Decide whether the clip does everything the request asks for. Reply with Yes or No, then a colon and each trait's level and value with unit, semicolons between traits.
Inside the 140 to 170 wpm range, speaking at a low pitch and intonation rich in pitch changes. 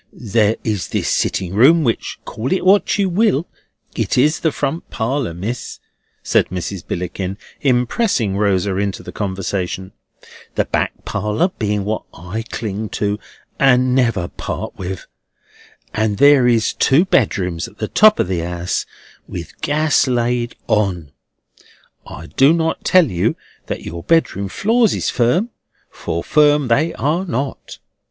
Yes: average, 145 wpm; low, 115 Hz; wide, 7.2 semitones